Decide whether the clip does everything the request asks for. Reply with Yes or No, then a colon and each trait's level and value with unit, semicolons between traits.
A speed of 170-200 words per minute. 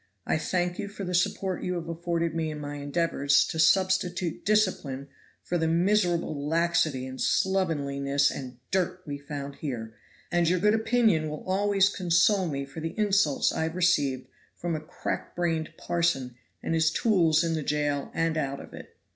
Yes: average, 175 wpm